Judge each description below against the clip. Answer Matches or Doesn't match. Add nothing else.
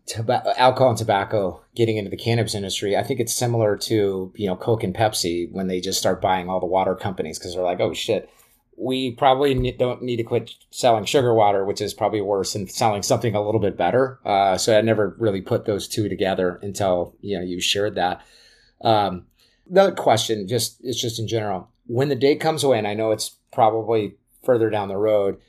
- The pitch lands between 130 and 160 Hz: Doesn't match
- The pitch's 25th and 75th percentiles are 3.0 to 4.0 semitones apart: Matches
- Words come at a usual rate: Doesn't match